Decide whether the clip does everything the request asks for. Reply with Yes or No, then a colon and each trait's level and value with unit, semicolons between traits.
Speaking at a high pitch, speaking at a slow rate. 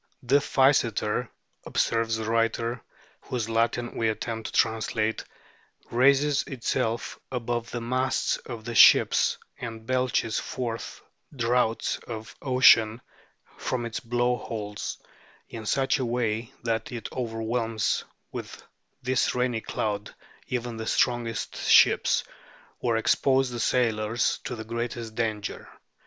No: low, 115 Hz; slow, 125 wpm